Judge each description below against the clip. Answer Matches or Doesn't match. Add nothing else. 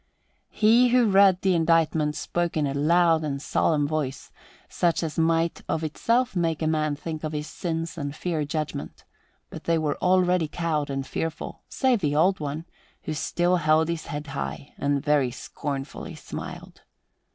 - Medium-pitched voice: Matches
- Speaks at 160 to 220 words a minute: Matches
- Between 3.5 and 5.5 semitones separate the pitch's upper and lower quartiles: Doesn't match